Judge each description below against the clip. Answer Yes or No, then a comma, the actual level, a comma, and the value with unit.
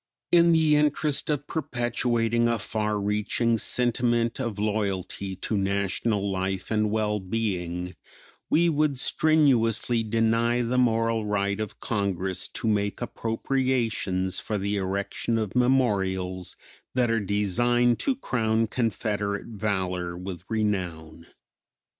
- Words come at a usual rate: No, slow, 115 wpm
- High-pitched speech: No, low, 110 Hz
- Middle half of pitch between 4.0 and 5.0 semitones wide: No, average, 3.4 semitones